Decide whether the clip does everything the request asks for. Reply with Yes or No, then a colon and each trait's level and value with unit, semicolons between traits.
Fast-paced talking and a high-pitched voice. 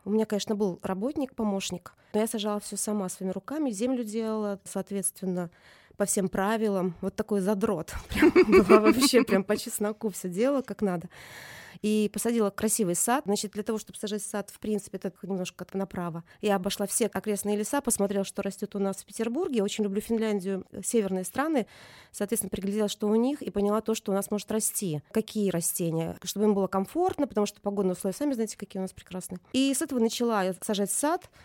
Yes: fast, 190 wpm; high, 205 Hz